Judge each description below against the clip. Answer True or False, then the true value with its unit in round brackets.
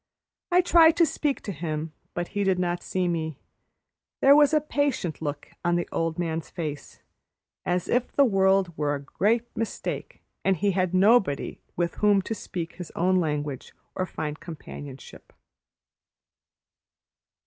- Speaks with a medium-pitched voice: True (180 Hz)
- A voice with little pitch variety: False (4.6 semitones)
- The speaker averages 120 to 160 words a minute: True (150 wpm)